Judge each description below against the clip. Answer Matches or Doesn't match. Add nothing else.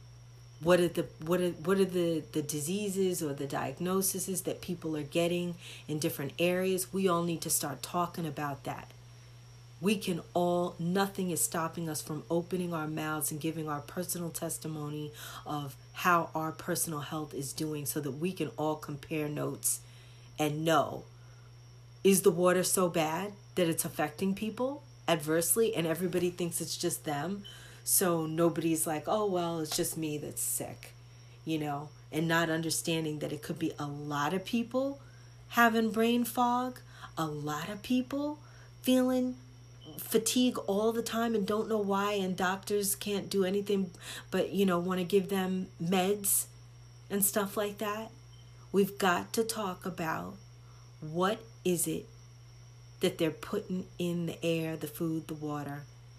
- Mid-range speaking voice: Matches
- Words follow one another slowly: Doesn't match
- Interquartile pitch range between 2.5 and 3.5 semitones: Doesn't match